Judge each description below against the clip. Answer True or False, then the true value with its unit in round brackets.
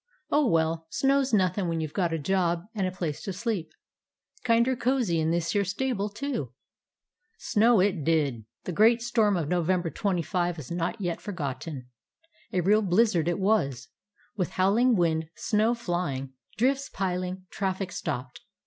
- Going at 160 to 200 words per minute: True (165 wpm)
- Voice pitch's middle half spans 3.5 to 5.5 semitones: True (4.7 semitones)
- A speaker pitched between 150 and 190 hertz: True (185 Hz)